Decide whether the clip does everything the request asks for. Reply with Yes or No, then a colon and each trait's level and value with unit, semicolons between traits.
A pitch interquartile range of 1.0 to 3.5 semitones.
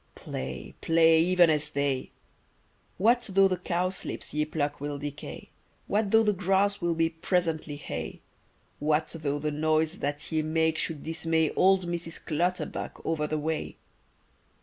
Yes: average, 2.9 semitones